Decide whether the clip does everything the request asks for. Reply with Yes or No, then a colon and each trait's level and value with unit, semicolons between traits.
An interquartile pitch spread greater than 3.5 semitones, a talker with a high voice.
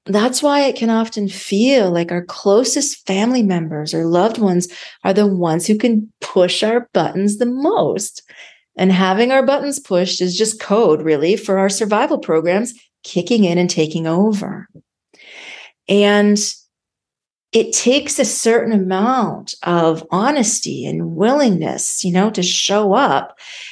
Yes: average, 4.7 semitones; high, 205 Hz